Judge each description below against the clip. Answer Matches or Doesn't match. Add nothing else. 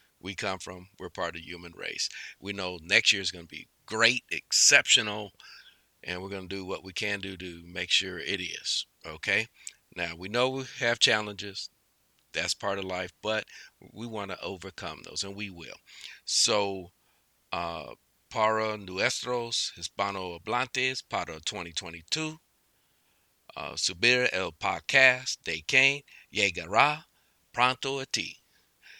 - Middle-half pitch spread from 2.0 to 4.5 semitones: Doesn't match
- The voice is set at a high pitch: Doesn't match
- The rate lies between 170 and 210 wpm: Doesn't match